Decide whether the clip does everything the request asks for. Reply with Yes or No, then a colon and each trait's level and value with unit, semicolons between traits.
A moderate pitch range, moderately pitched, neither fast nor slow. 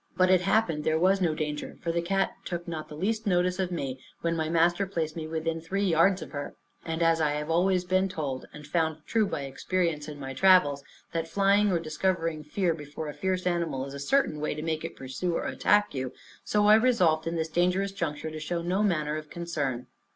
No: average, 3.2 semitones; medium, 165 Hz; fast, 225 wpm